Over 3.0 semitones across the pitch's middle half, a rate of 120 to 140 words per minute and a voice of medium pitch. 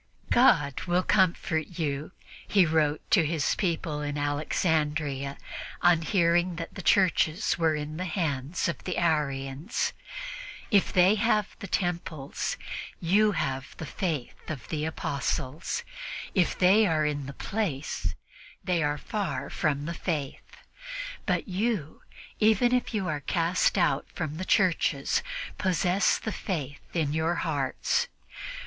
Yes: average, 4.0 semitones; slow, 135 wpm; medium, 165 Hz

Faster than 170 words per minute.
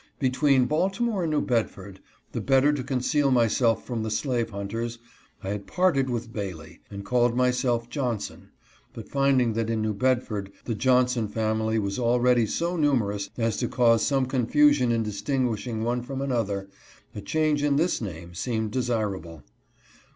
No: average, 160 wpm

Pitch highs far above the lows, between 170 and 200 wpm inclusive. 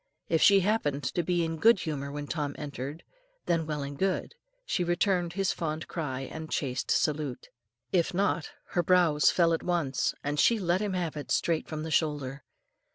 No: average, 3.3 semitones; average, 185 wpm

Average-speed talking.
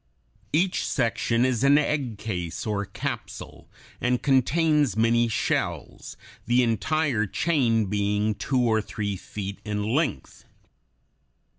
No: slow, 115 wpm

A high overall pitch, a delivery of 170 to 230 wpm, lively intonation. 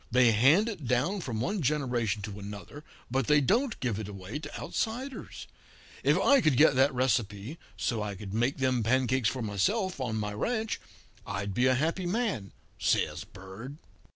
No: low, 130 Hz; average, 175 wpm; wide, 6.7 semitones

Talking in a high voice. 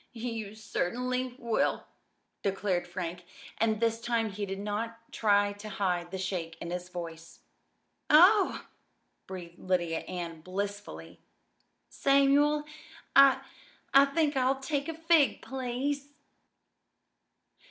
Yes: high, 220 Hz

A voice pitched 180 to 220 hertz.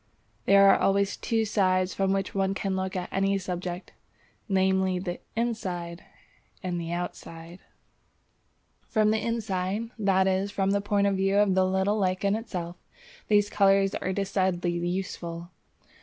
Yes: high, 190 Hz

